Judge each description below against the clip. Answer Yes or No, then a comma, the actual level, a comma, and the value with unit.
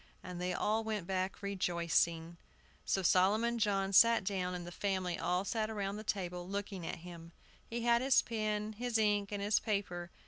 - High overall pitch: Yes, high, 195 Hz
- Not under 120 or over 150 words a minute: No, average, 180 wpm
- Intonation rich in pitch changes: No, average, 3.1 semitones